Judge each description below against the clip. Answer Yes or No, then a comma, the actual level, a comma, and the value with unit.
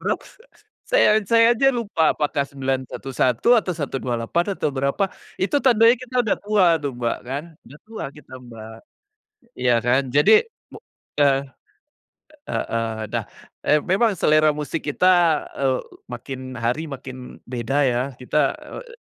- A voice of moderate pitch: Yes, medium, 145 Hz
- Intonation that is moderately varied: No, wide, 7.5 semitones